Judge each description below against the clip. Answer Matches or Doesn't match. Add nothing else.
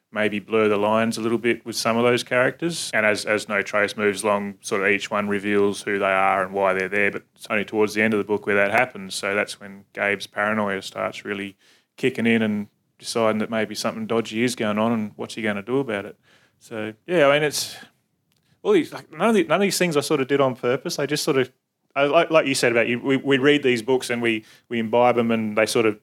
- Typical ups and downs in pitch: Matches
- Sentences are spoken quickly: Matches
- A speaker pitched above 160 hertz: Doesn't match